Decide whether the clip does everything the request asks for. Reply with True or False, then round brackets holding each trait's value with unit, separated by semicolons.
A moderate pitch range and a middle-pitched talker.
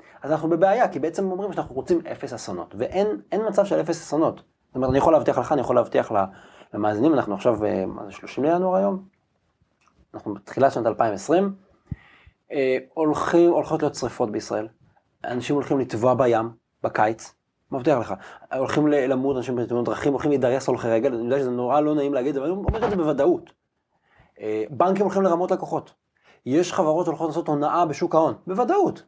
False (5.7 semitones; 150 Hz)